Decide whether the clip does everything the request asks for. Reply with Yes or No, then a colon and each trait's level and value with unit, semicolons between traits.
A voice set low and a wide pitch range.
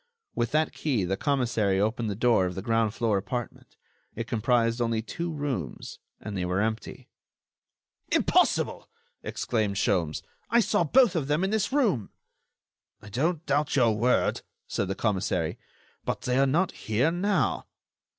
Yes: low, 120 Hz; wide, 6.3 semitones